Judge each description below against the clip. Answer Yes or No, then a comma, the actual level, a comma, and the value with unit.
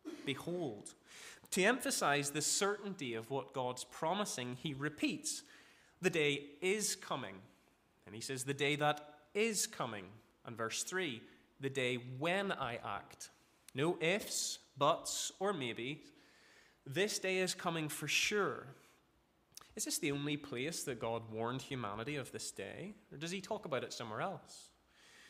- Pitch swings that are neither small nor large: No, wide, 7.0 semitones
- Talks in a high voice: No, medium, 150 Hz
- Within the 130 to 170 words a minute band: Yes, average, 145 wpm